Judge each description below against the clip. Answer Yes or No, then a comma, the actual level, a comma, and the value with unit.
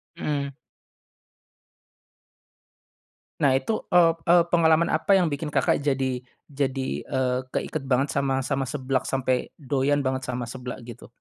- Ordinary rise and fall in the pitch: No, narrow, 2.2 semitones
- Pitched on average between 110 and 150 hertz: Yes, low, 135 Hz